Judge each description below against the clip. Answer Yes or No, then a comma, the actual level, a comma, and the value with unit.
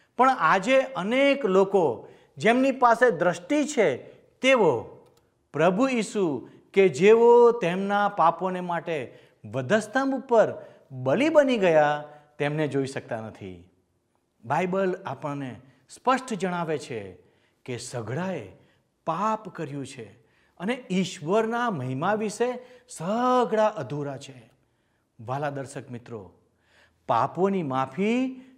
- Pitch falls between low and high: Yes, medium, 180 Hz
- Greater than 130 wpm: No, average, 95 wpm